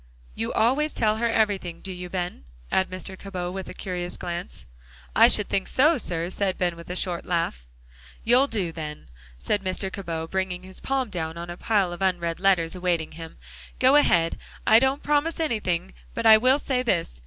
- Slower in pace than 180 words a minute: No, average, 190 wpm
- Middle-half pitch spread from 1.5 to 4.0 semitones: No, average, 4.4 semitones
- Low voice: No, medium, 185 Hz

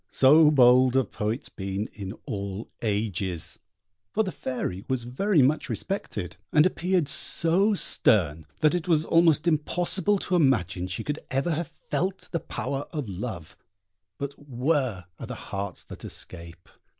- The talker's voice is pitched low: Yes, low, 130 Hz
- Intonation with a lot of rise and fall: Yes, wide, 8.5 semitones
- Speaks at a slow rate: No, average, 150 wpm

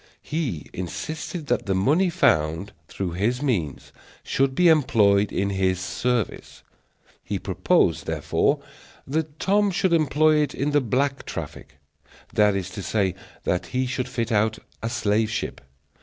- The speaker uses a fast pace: No, average, 145 wpm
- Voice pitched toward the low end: Yes, low, 120 Hz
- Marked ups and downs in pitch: Yes, wide, 7.0 semitones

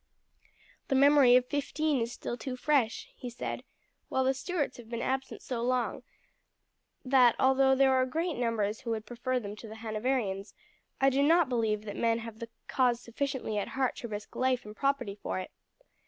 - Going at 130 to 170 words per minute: No, average, 185 wpm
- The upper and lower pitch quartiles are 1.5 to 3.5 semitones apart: Yes, average, 2.8 semitones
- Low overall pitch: No, very high, 250 Hz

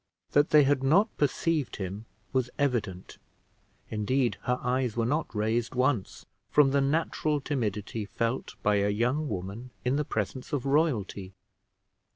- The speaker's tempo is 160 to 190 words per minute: No, average, 145 wpm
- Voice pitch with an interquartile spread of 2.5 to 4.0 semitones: No, average, 5.2 semitones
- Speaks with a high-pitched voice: No, low, 125 Hz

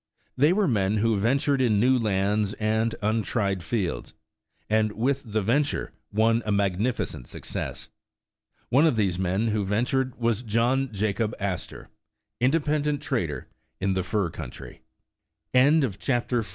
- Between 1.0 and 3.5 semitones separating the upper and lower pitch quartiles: No, average, 4.3 semitones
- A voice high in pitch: No, low, 110 Hz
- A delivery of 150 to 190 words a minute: No, average, 140 wpm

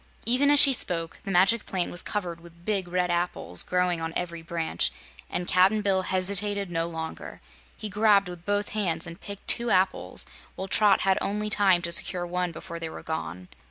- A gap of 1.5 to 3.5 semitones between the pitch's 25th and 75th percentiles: Yes, average, 3.1 semitones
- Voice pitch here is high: No, medium, 180 Hz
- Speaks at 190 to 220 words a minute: Yes, average, 195 wpm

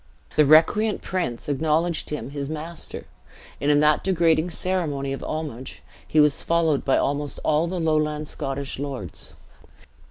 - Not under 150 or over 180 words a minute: No, average, 140 wpm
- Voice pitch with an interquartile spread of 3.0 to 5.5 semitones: No, narrow, 2.6 semitones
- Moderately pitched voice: Yes, medium, 150 Hz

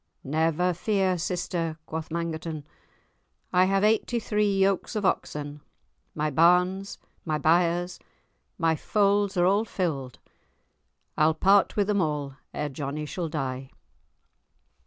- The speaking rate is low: Yes, slow, 120 wpm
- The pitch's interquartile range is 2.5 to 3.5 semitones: No, average, 4.1 semitones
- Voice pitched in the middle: Yes, medium, 170 Hz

